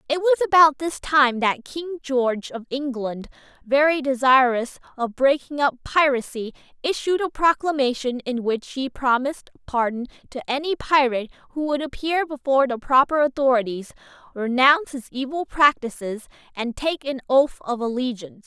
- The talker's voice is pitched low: No, very high, 270 Hz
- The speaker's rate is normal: Yes, average, 145 wpm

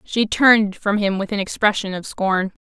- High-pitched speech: Yes, high, 205 Hz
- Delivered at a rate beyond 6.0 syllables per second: No, 4.9 syllables/s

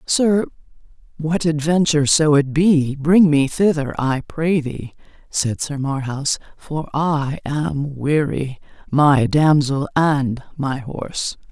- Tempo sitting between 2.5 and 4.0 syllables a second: Yes, 3.6 syllables/s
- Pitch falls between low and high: Yes, medium, 150 Hz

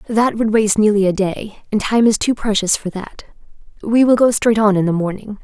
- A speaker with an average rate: No, fast, 230 wpm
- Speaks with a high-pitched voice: Yes, high, 210 Hz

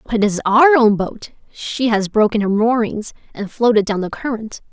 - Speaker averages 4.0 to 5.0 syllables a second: Yes, 4.9 syllables/s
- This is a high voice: Yes, high, 220 Hz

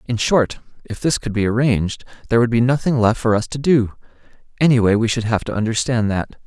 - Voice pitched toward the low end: Yes, low, 115 Hz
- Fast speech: Yes, fast, 215 wpm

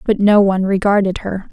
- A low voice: No, high, 200 Hz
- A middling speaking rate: Yes, average, 195 wpm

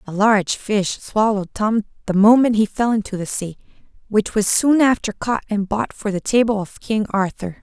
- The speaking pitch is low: No, high, 210 Hz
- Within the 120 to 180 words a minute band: No, average, 195 wpm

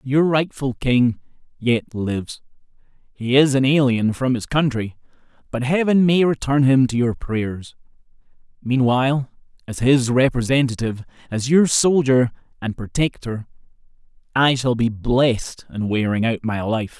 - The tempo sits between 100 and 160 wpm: Yes, slow, 135 wpm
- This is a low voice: Yes, low, 125 Hz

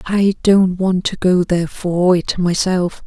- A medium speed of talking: Yes, average, 175 wpm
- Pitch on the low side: No, medium, 180 Hz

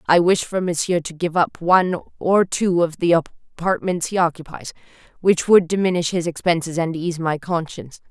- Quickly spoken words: No, average, 180 wpm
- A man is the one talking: No, female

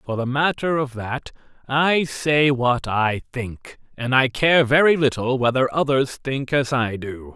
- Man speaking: Yes, male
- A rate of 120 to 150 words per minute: No, average, 170 wpm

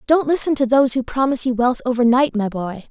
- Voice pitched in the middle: No, very high, 250 Hz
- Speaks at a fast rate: Yes, fast, 225 wpm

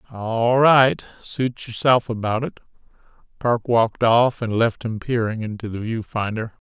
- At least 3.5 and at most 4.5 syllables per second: Yes, 4.3 syllables/s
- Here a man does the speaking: Yes, male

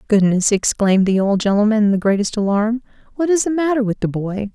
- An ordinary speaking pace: No, fast, 210 wpm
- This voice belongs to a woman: Yes, female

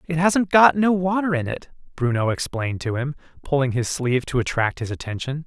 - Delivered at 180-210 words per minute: Yes, average, 200 wpm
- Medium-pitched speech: Yes, medium, 145 Hz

